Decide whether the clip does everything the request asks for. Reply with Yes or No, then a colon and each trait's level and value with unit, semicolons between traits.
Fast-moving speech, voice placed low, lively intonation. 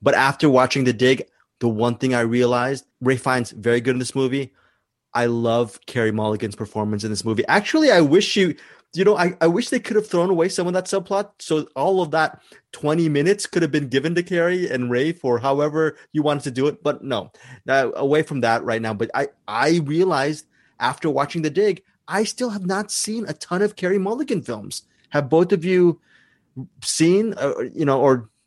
No: fast, 210 wpm; medium, 150 Hz; wide, 6.2 semitones